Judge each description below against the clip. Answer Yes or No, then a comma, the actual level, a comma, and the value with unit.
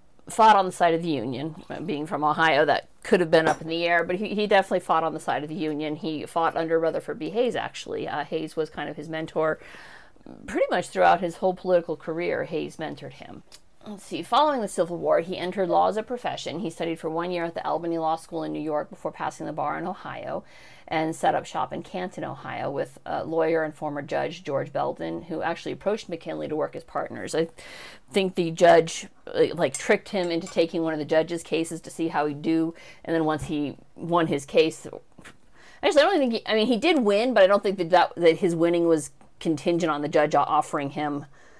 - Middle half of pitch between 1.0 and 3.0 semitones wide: Yes, narrow, 2.5 semitones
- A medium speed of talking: No, fast, 230 wpm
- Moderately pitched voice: Yes, medium, 165 Hz